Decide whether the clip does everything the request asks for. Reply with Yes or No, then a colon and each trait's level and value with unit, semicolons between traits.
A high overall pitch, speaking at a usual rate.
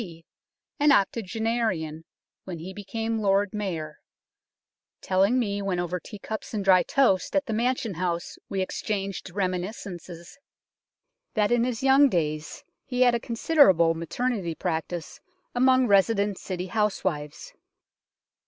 No: high, 195 Hz; slow, 125 wpm